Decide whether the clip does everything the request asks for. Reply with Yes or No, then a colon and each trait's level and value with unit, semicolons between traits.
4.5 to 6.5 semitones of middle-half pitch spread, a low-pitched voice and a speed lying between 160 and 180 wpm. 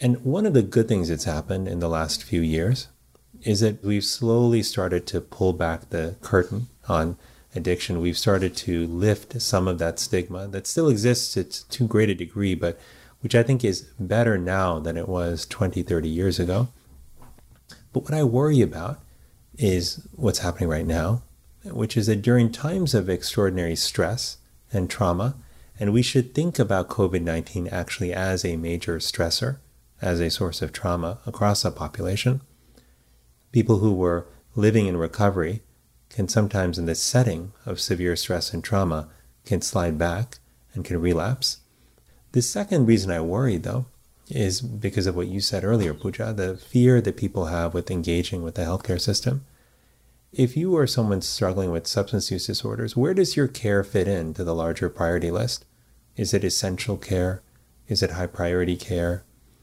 Yes: average, 5.1 semitones; very low, 95 Hz; average, 170 wpm